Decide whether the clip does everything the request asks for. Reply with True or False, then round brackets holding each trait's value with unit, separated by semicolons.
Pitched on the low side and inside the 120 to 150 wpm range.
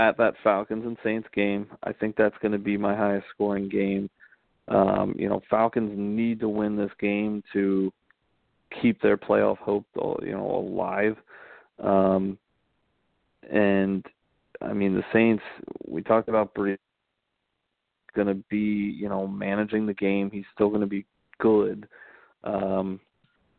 True (100 Hz; 140 wpm)